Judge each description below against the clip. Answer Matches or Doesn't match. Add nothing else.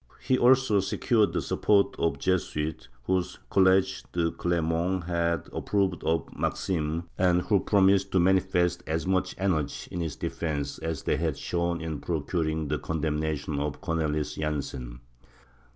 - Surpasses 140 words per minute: Matches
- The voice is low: Matches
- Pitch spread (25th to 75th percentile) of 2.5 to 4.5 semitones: Matches